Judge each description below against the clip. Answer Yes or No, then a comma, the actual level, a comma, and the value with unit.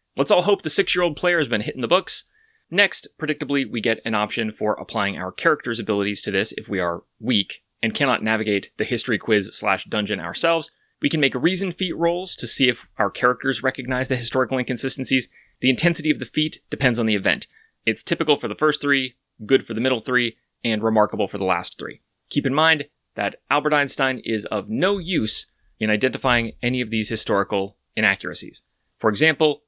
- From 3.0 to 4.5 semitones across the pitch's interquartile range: No, average, 5.3 semitones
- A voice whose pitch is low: Yes, low, 130 Hz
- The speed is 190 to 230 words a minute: Yes, average, 200 wpm